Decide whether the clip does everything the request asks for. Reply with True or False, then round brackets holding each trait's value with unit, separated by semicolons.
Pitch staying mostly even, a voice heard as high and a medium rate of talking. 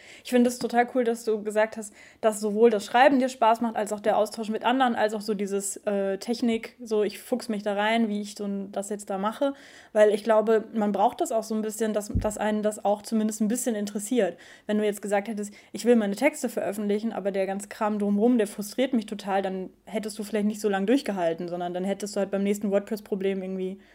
False (1.9 semitones; 215 Hz; 245 wpm)